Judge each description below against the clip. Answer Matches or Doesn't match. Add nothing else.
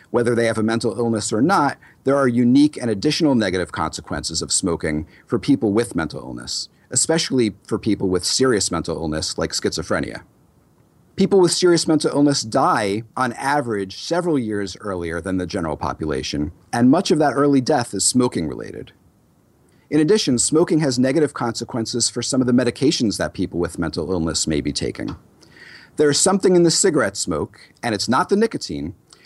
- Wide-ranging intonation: Matches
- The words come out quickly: Doesn't match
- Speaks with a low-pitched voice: Matches